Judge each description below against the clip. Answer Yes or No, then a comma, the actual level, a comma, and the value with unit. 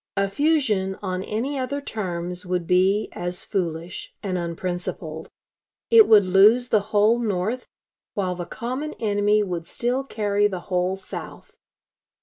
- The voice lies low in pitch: No, high, 200 Hz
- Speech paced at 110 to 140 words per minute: Yes, slow, 135 wpm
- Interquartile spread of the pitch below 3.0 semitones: No, average, 3.7 semitones